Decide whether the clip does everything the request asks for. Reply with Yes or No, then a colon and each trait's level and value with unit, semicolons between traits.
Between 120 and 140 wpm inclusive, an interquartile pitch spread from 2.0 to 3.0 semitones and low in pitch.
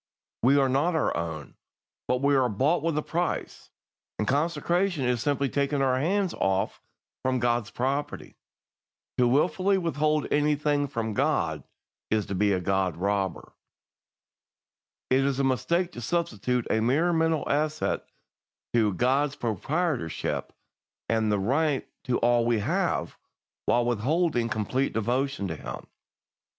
No: slow, 135 wpm; average, 5.1 semitones; low, 130 Hz